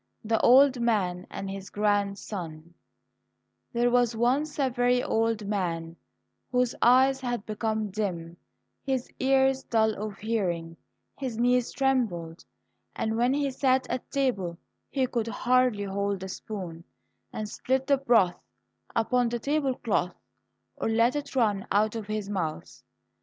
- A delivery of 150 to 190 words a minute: No, average, 140 wpm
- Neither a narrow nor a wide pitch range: Yes, average, 4.3 semitones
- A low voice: No, high, 225 Hz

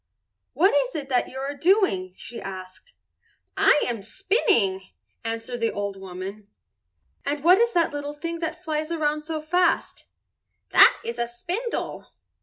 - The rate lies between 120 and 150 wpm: Yes, average, 145 wpm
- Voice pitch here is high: Yes, very high, 285 Hz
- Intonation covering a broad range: Yes, wide, 6.8 semitones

